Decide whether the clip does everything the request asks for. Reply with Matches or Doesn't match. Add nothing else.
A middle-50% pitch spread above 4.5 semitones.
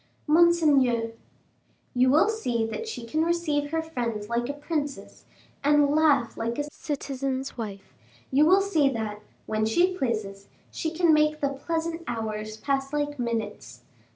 Matches